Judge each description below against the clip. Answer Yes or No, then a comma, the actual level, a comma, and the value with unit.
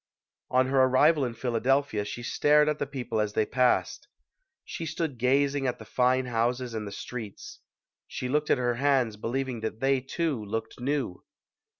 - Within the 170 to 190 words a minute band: Yes, average, 175 wpm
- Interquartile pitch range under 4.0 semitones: Yes, average, 3.3 semitones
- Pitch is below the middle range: Yes, low, 130 Hz